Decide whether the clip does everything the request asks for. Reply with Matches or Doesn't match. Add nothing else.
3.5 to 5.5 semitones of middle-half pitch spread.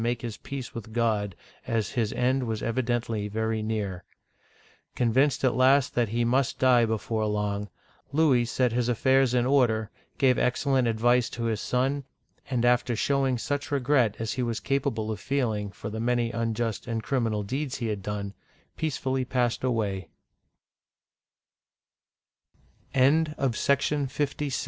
Doesn't match